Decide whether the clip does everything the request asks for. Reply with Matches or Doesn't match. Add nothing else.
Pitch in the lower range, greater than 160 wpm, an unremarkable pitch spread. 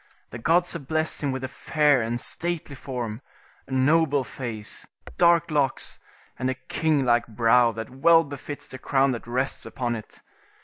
Matches